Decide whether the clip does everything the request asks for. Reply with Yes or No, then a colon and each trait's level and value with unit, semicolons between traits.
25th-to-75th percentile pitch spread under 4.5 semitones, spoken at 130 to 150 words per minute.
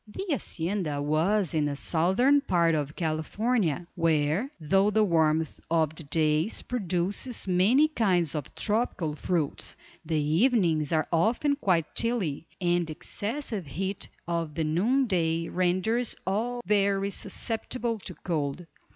No: average, 5.2 semitones; slow, 135 wpm